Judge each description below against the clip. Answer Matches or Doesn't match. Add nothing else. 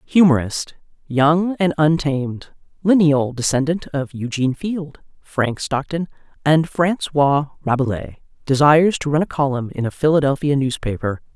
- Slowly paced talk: Matches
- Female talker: Matches